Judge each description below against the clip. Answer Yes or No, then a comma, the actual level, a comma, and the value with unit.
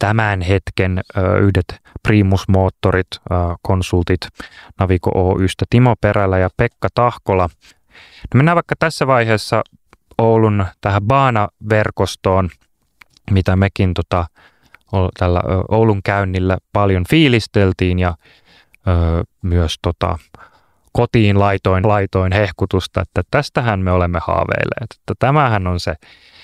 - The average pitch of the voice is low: Yes, very low, 95 Hz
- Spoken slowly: No, average, 105 wpm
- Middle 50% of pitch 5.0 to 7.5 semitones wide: No, average, 2.9 semitones